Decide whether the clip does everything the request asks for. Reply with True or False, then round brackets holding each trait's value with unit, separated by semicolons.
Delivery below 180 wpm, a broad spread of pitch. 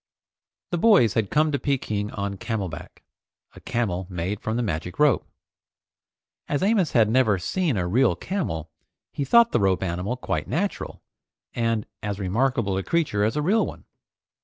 True (165 wpm; 7.2 semitones)